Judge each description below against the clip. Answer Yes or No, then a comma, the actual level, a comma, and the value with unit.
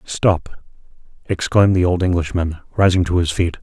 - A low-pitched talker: Yes, very low, 90 Hz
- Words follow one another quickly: No, average, 150 wpm